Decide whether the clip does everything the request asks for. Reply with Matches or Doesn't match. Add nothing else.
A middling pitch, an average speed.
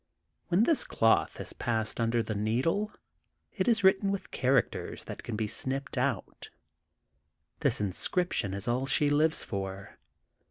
Doesn't match